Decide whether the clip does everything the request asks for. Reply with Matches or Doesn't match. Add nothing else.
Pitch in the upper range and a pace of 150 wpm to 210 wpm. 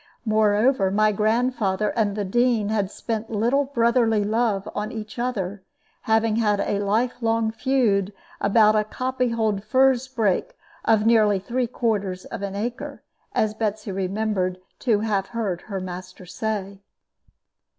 Doesn't match